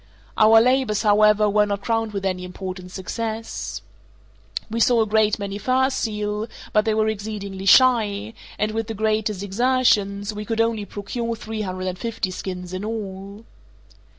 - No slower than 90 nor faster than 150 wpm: No, average, 160 wpm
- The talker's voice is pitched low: No, high, 210 Hz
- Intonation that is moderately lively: No, narrow, 2.1 semitones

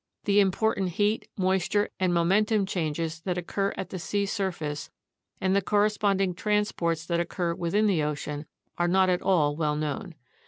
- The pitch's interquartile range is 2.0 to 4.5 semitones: Yes, average, 3.2 semitones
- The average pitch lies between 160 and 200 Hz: Yes, medium, 185 Hz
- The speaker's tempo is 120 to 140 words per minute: No, average, 160 wpm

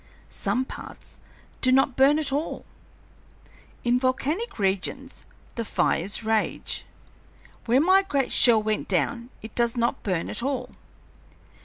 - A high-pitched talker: Yes, high, 245 Hz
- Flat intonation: No, average, 3.7 semitones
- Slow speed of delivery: Yes, slow, 130 wpm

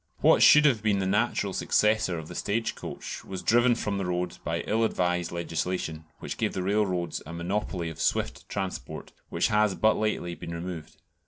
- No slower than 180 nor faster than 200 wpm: Yes, average, 185 wpm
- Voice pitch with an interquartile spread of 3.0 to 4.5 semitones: Yes, average, 3.5 semitones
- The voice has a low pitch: Yes, very low, 95 Hz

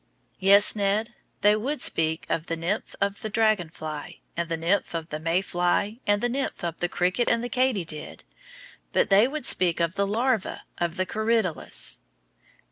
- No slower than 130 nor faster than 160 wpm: No, average, 180 wpm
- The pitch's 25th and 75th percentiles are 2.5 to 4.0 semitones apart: No, average, 4.5 semitones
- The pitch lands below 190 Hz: No, high, 195 Hz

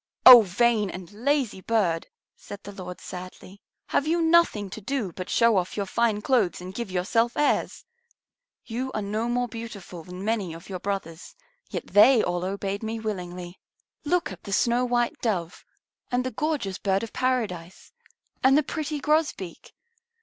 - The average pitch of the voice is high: Yes, high, 215 Hz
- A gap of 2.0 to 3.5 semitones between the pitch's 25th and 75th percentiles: No, average, 4.9 semitones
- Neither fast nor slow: Yes, average, 165 wpm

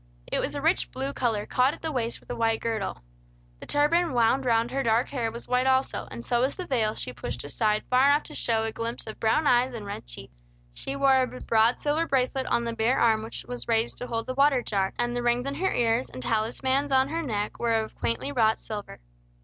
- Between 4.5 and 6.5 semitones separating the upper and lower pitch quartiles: No, average, 3.0 semitones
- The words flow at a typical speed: No, fast, 240 wpm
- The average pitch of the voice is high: Yes, high, 240 Hz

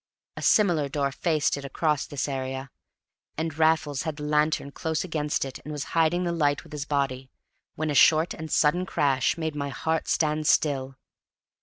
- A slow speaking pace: No, average, 180 wpm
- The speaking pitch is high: No, medium, 150 Hz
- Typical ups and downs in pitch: No, narrow, 2.2 semitones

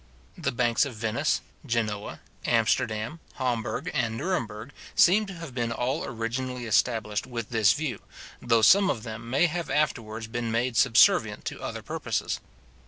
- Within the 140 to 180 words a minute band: Yes, average, 150 wpm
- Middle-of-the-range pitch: No, low, 120 Hz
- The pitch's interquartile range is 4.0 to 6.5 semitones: No, average, 3.4 semitones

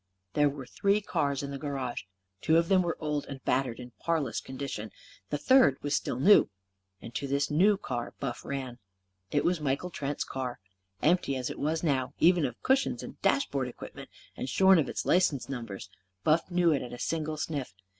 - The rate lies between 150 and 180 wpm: No, average, 195 wpm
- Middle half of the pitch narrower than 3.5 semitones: No, average, 4.2 semitones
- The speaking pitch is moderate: Yes, medium, 145 Hz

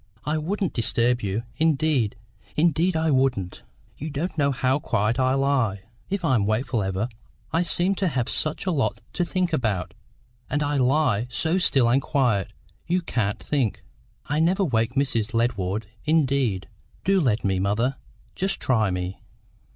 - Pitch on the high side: No, low, 135 Hz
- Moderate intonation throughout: No, wide, 6.1 semitones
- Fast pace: No, average, 160 wpm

